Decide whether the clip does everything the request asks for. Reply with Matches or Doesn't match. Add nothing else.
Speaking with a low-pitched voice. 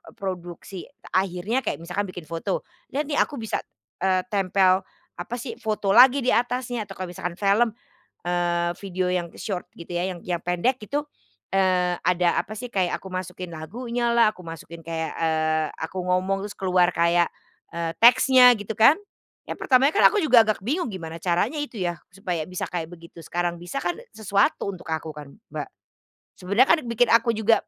Doesn't match